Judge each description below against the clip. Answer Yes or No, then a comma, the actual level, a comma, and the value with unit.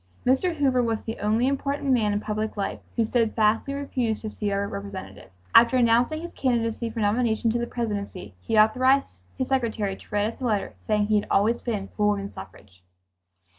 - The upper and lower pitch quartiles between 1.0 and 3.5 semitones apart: Yes, average, 3.2 semitones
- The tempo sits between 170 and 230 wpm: Yes, average, 190 wpm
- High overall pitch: Yes, high, 225 Hz